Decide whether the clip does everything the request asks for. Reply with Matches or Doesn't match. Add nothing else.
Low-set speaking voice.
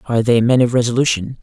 Matches